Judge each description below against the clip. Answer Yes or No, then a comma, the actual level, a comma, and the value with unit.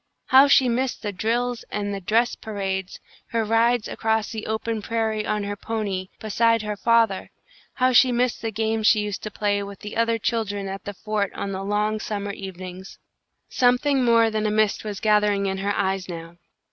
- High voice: Yes, high, 215 Hz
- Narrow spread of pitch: Yes, narrow, 2.2 semitones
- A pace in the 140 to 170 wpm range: No, average, 190 wpm